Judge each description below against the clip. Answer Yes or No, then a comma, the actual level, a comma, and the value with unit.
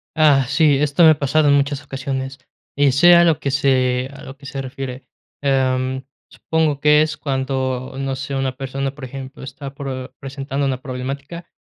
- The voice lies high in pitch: No, low, 135 Hz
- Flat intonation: Yes, narrow, 1.4 semitones